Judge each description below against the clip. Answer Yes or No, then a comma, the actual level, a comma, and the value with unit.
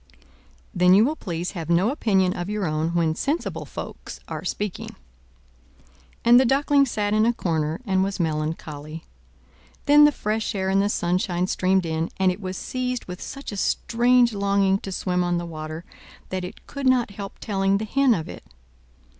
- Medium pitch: No, high, 195 Hz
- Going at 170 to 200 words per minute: Yes, average, 180 wpm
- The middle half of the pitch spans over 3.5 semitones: Yes, average, 4.7 semitones